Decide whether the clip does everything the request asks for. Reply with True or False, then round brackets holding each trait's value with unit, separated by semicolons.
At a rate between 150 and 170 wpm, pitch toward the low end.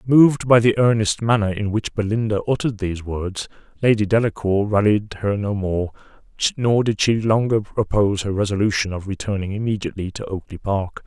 True (165 wpm; 105 Hz)